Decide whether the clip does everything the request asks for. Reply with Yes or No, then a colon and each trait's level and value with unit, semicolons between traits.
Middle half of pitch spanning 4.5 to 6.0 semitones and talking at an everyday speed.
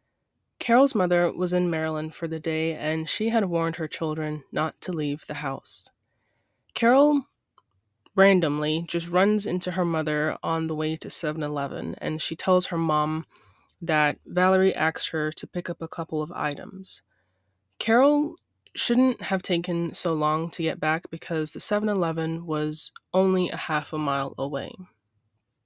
No: average, 3.2 semitones; average, 160 wpm